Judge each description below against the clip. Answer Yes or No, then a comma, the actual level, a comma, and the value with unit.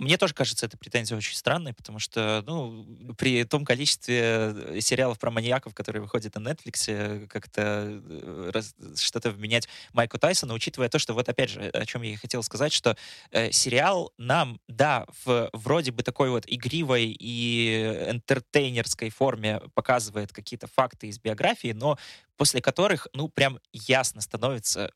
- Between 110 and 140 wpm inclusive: No, average, 155 wpm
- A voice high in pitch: No, low, 120 Hz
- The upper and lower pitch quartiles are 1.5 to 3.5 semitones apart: Yes, average, 3.2 semitones